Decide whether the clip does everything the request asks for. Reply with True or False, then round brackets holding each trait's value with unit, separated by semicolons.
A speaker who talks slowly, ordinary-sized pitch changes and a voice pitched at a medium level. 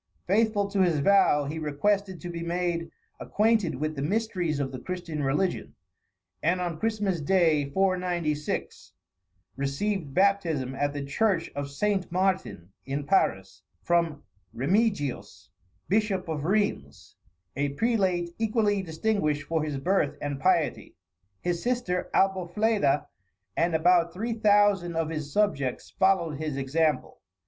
True (130 wpm; 5.0 semitones; 175 Hz)